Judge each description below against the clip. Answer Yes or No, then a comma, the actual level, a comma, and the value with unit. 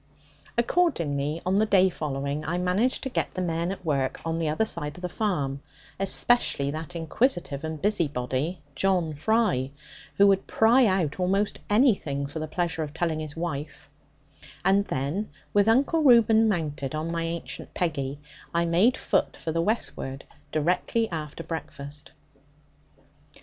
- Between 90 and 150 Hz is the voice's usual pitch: No, medium, 170 Hz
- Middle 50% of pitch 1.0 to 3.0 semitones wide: No, average, 5.1 semitones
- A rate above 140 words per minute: Yes, average, 150 wpm